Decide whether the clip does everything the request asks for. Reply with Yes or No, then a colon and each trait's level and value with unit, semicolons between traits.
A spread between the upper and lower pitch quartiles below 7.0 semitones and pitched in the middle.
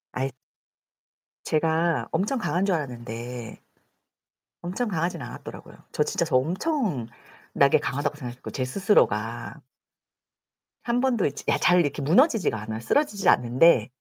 No: wide, 7.9 semitones; medium, 155 Hz